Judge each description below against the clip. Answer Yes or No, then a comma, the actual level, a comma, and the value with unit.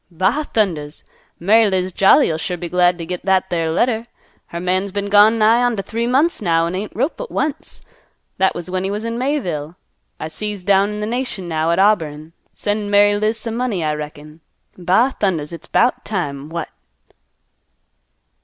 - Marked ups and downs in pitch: No, average, 4.5 semitones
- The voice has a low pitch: No, high, 190 Hz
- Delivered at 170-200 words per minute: Yes, average, 185 wpm